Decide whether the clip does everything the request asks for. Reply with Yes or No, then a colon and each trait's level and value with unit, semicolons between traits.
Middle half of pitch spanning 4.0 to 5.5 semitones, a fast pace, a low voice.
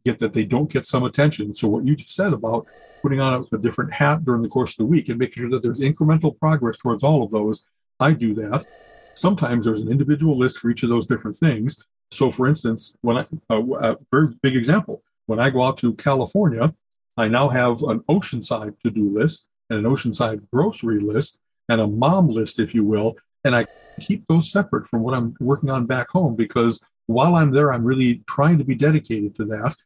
Yes: average, 4.7 semitones; fast, 215 wpm; low, 130 Hz